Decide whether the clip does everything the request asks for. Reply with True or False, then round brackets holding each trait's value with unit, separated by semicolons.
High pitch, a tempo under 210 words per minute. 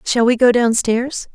False (240 Hz; 225 wpm)